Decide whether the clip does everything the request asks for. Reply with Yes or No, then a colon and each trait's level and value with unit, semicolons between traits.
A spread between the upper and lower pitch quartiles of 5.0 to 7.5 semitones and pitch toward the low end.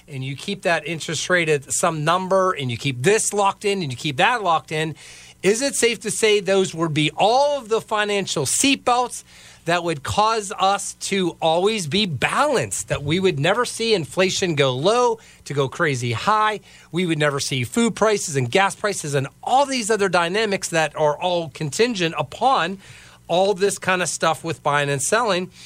No: average, 5.3 semitones; medium, 180 Hz